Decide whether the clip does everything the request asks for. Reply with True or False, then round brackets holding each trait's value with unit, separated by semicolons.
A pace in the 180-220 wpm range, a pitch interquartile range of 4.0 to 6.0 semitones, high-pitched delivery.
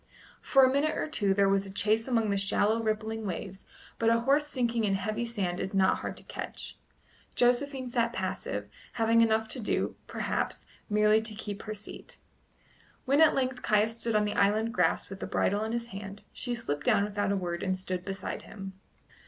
False (200 wpm; 3.1 semitones; 215 Hz)